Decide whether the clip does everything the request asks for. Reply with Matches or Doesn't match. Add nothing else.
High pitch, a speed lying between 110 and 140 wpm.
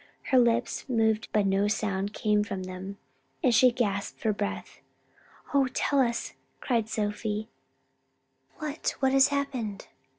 Matches